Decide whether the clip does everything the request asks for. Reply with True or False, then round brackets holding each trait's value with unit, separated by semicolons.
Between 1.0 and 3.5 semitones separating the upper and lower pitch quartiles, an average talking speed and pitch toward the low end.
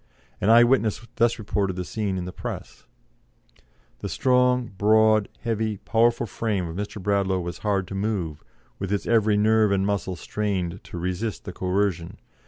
True (2.9 semitones; 165 wpm; 105 Hz)